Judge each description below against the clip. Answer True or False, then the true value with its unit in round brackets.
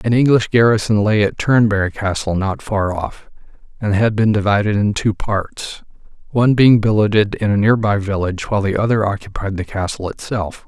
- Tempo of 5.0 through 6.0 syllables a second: True (5.3 syllables/s)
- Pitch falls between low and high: False (105 Hz)